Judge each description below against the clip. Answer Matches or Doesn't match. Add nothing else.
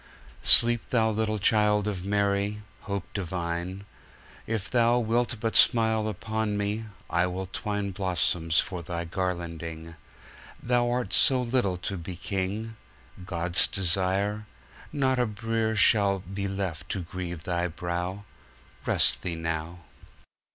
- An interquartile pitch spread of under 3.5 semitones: Doesn't match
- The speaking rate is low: Matches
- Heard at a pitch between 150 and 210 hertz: Doesn't match